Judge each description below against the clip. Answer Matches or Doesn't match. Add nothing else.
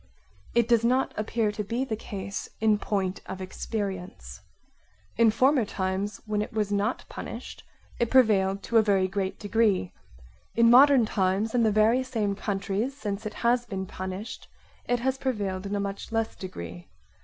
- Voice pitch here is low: Doesn't match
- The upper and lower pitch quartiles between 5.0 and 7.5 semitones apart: Doesn't match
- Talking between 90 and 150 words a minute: Doesn't match